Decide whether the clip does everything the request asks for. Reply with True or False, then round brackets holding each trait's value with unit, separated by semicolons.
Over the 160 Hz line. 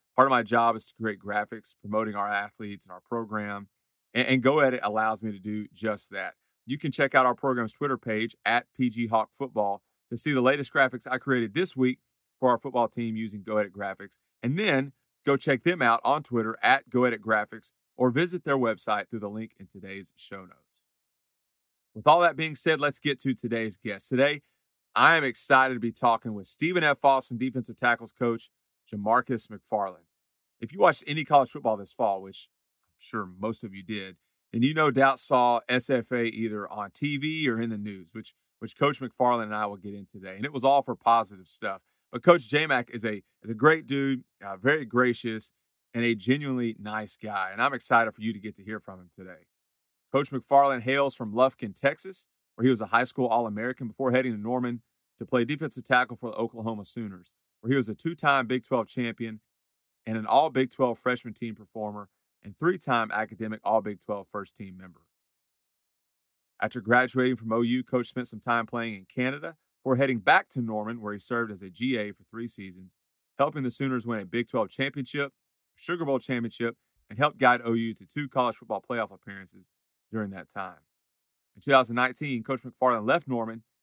False (120 Hz)